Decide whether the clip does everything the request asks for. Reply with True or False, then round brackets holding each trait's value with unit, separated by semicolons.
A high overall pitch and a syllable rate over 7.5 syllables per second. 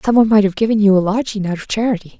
True (210 Hz; 7.7 syllables/s)